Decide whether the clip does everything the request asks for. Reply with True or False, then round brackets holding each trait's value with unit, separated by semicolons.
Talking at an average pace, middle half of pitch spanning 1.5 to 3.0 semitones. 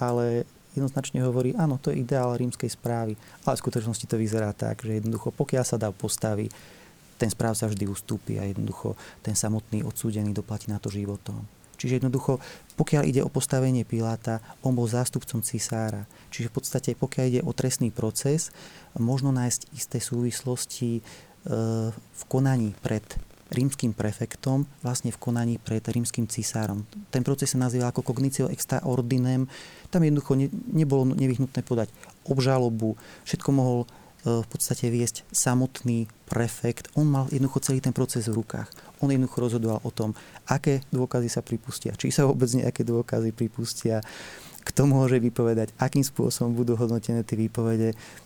True (155 wpm; 2.7 semitones)